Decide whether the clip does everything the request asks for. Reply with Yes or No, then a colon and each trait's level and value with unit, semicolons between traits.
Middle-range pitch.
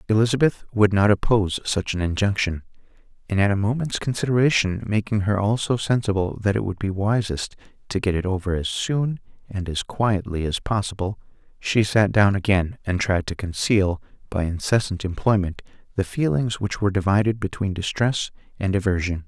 No: low, 100 Hz